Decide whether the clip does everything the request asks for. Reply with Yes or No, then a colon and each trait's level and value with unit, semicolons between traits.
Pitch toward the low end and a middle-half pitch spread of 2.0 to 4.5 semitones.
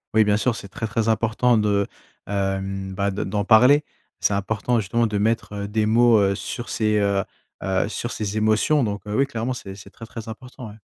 Yes: low, 110 Hz; narrow, 2.4 semitones